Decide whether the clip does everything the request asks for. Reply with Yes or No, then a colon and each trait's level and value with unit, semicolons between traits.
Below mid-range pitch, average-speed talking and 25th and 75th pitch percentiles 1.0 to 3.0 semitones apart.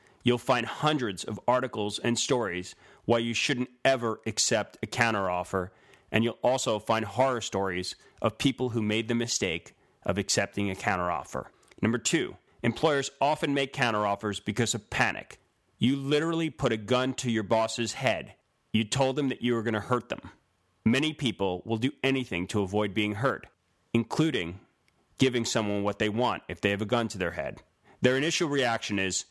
No: low, 115 Hz; average, 175 wpm; average, 3.7 semitones